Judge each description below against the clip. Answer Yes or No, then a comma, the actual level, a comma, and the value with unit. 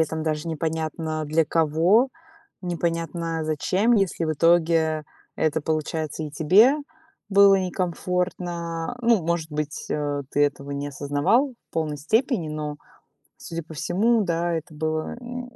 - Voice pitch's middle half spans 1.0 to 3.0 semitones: Yes, average, 2.7 semitones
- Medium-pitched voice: Yes, medium, 165 Hz